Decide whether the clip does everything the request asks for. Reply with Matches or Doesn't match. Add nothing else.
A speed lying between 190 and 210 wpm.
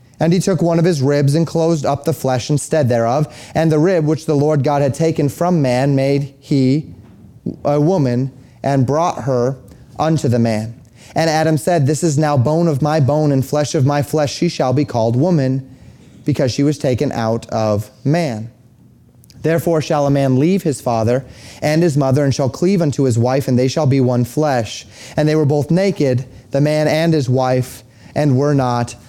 Matches